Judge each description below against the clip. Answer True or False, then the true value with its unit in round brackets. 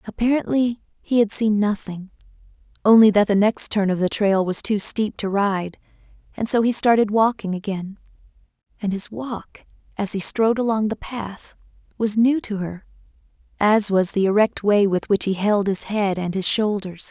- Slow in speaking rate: False (175 wpm)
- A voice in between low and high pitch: False (205 Hz)